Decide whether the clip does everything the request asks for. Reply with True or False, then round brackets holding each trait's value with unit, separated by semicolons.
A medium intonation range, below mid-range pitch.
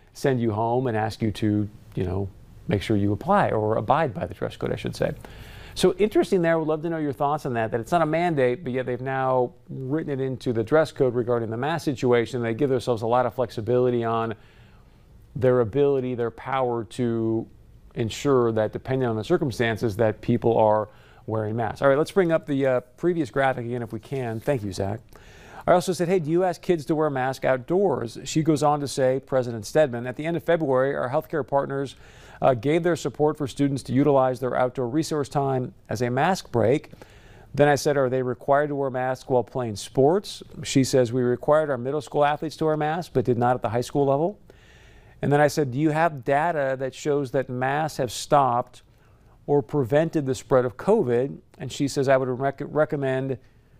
True (3.6 semitones; 130 Hz)